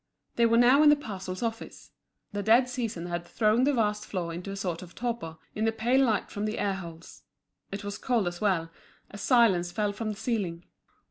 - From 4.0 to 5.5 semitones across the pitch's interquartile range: Yes, average, 4.3 semitones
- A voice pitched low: No, high, 210 Hz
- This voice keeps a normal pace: No, fast, 210 wpm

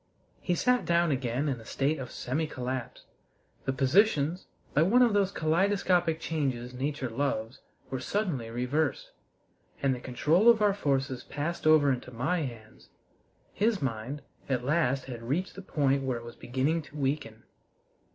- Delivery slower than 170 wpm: Yes, average, 160 wpm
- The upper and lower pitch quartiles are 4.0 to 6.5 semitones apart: Yes, average, 5.1 semitones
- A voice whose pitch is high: No, medium, 140 Hz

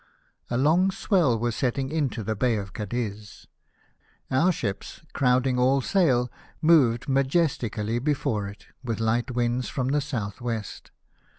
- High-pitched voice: No, low, 125 Hz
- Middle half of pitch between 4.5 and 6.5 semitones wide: No, average, 3.6 semitones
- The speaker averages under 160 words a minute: Yes, slow, 135 wpm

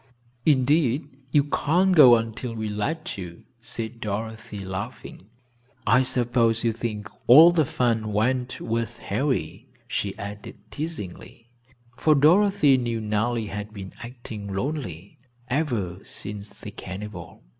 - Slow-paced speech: Yes, slow, 125 wpm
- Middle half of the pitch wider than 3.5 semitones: Yes, average, 4.4 semitones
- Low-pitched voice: Yes, low, 115 Hz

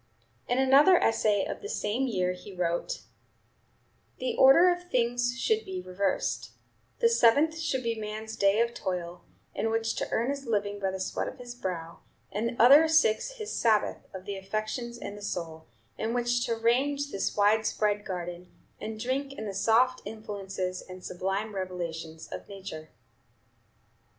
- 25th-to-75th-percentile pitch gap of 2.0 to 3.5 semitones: No, average, 4.9 semitones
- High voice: Yes, high, 220 Hz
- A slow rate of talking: No, average, 165 wpm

